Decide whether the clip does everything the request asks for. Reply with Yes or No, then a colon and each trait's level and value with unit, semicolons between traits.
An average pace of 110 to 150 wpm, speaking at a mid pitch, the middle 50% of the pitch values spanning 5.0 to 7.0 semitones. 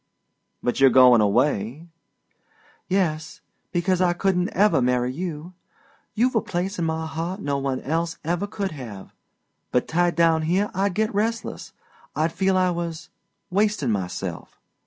Yes: average, 145 wpm; medium, 170 Hz; average, 5.3 semitones